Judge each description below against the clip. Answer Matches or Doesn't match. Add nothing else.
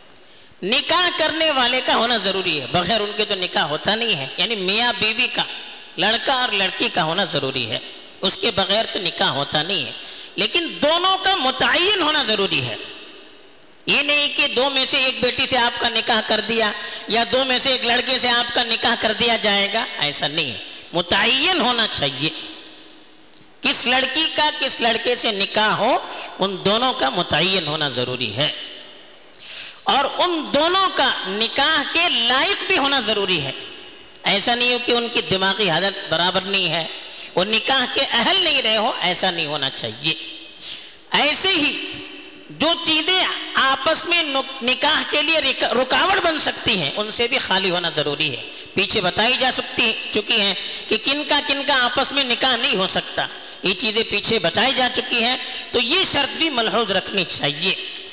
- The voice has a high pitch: Matches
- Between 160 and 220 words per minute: Matches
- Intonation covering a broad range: Matches